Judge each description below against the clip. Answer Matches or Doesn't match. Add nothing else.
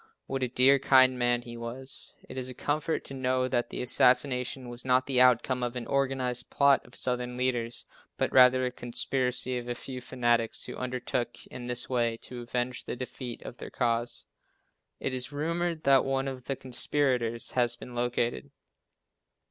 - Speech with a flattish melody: Matches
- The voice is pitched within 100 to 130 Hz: Matches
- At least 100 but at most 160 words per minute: Doesn't match